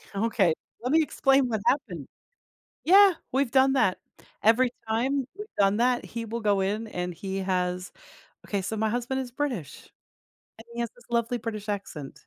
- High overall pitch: Yes, high, 230 Hz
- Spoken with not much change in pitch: No, average, 4.6 semitones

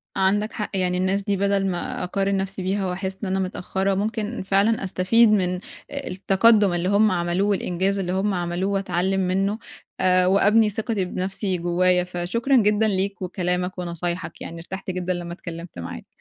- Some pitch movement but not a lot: No, narrow, 1.9 semitones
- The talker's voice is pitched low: No, high, 190 Hz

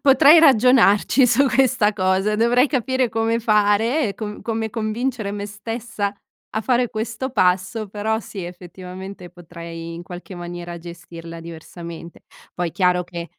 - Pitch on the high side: Yes, high, 205 Hz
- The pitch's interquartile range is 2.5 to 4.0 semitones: No, average, 4.6 semitones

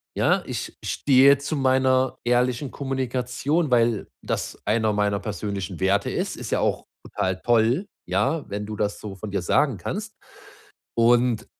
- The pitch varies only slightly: No, average, 4.3 semitones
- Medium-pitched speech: No, low, 120 Hz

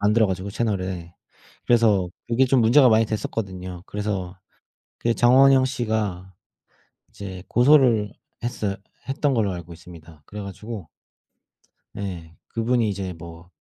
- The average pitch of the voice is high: No, low, 105 Hz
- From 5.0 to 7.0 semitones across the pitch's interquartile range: No, average, 4.3 semitones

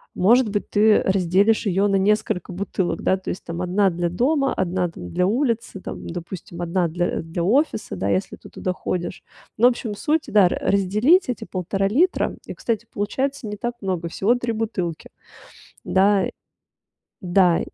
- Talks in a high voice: Yes, high, 195 Hz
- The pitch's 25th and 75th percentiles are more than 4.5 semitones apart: No, average, 4.0 semitones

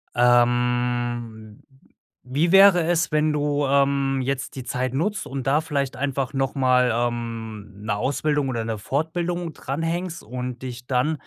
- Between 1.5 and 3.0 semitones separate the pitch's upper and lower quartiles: No, average, 3.6 semitones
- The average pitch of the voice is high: No, low, 135 Hz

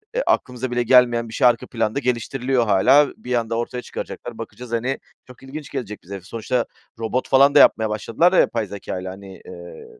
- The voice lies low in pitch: Yes, low, 120 Hz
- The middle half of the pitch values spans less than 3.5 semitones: Yes, average, 2.9 semitones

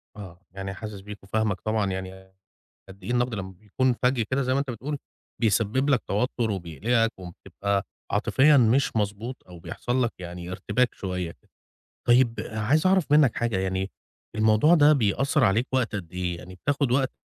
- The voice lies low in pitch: Yes, low, 110 Hz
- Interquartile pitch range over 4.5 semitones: Yes, average, 5.2 semitones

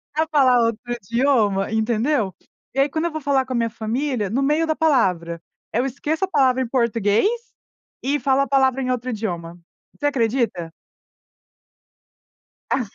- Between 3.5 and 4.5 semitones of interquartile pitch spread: Yes, average, 4.2 semitones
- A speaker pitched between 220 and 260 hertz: Yes, very high, 250 Hz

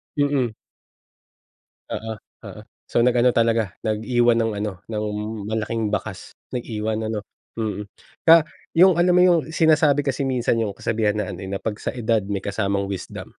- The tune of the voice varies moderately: Yes, average, 3.5 semitones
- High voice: No, low, 115 Hz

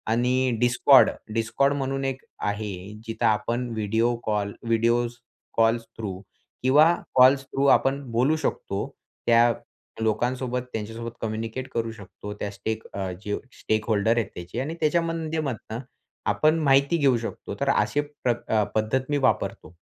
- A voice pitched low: Yes, low, 115 Hz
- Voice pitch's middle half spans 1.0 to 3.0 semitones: No, average, 3.4 semitones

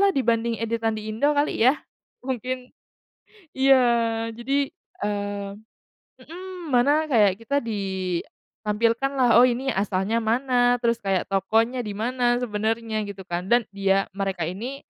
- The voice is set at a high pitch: Yes, high, 230 Hz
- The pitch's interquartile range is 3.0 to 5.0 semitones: Yes, average, 3.9 semitones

